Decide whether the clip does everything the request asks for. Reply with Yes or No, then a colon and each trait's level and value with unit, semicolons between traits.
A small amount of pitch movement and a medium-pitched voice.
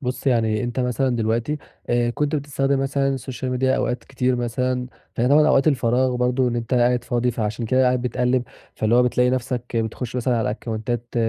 No: narrow, 1.5 semitones; low, 125 Hz